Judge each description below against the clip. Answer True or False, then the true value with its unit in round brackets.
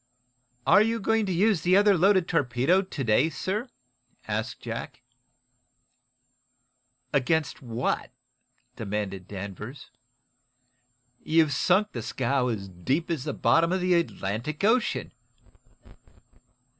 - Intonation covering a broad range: True (7.7 semitones)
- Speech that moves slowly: True (110 wpm)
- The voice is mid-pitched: True (160 Hz)